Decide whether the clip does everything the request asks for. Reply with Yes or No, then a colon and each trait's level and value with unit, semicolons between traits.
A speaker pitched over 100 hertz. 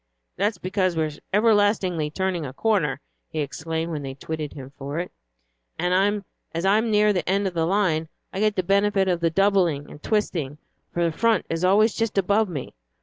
Yes: medium, 185 Hz